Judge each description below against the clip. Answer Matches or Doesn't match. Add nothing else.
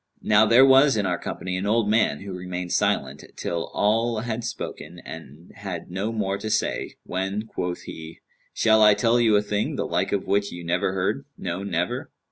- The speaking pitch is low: Matches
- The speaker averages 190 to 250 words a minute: Matches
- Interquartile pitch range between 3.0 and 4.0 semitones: Matches